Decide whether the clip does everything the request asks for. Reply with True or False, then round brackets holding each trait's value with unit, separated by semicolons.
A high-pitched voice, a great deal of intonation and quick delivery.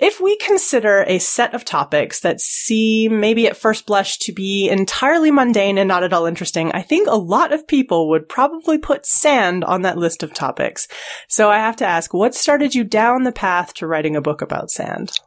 True (220 Hz; 7.1 semitones; 210 wpm)